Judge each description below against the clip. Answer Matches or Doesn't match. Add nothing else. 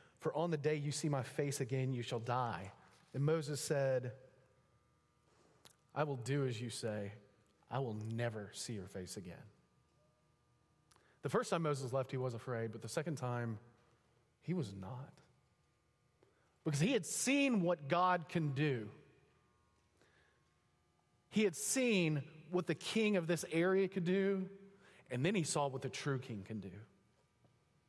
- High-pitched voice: Doesn't match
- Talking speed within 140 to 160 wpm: Matches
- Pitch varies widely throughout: Matches